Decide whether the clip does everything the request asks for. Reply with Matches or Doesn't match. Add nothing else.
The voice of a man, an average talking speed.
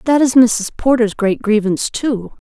Doesn't match